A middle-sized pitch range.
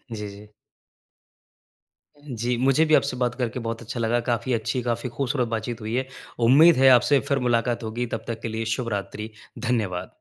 No: narrow, 2.2 semitones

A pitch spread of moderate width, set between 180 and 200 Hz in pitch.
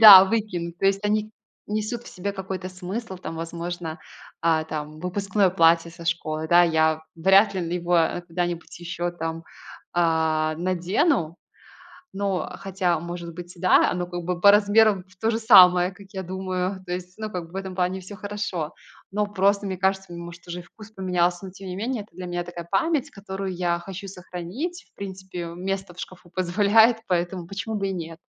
No: narrow, 2.3 semitones; medium, 185 Hz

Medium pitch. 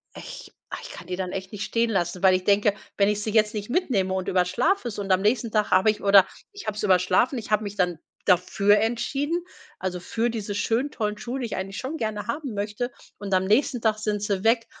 No: high, 210 Hz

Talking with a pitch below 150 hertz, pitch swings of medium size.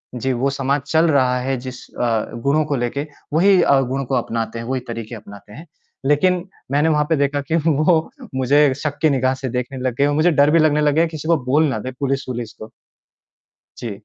Yes: medium, 140 Hz; average, 3.1 semitones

